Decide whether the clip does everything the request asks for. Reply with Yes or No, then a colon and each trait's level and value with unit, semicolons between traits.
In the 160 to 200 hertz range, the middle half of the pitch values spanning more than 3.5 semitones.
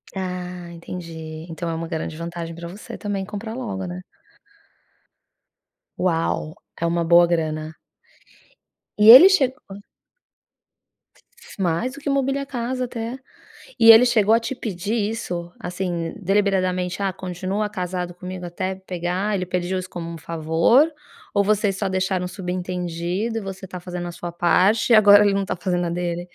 No: medium, 185 Hz; average, 3.2 semitones